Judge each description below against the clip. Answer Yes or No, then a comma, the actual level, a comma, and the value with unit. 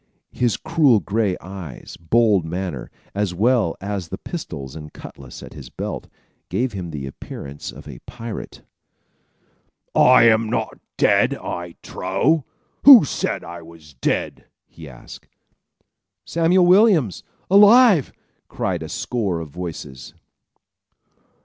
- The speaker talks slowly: Yes, slow, 125 wpm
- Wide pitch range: Yes, wide, 7.7 semitones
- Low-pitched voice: Yes, very low, 95 Hz